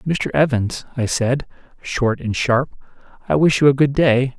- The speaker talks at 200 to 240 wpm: No, average, 180 wpm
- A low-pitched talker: Yes, low, 130 Hz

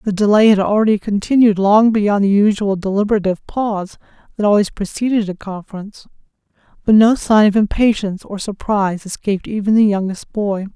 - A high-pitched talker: Yes, high, 205 Hz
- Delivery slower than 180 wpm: Yes, average, 155 wpm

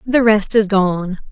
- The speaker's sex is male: No, female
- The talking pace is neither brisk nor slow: Yes, average, 180 wpm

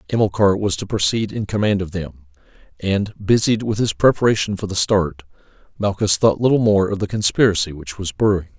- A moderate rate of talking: Yes, average, 180 wpm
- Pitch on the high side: No, low, 100 Hz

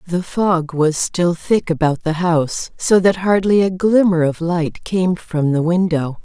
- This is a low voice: No, medium, 175 Hz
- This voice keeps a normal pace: Yes, average, 185 wpm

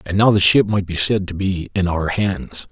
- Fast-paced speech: Yes, fast, 265 wpm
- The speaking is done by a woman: No, male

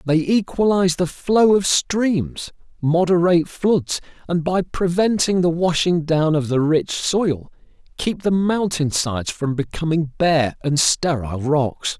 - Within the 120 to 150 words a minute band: Yes, average, 140 wpm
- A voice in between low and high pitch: Yes, medium, 165 Hz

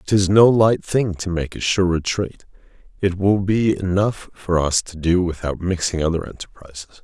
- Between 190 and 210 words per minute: No, average, 180 wpm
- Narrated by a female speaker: No, male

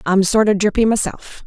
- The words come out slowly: No, fast, 205 wpm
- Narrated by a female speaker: Yes, female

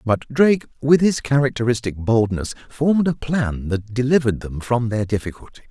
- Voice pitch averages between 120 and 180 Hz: Yes, low, 125 Hz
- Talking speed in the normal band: Yes, average, 160 wpm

